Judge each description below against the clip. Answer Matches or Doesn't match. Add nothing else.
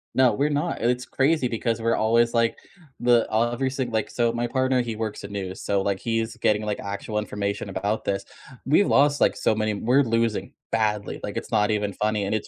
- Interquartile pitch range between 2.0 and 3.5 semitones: Matches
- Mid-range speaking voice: Doesn't match